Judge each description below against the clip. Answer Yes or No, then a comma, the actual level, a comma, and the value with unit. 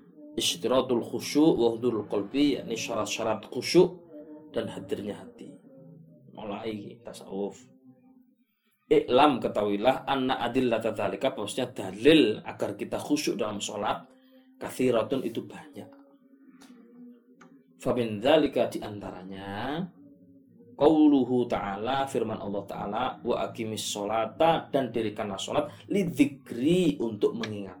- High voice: No, low, 135 Hz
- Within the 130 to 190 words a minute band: No, average, 95 wpm